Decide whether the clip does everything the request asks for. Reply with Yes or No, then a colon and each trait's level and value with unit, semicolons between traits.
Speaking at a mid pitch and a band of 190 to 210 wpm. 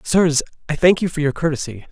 No: medium, 155 Hz; fast, 220 wpm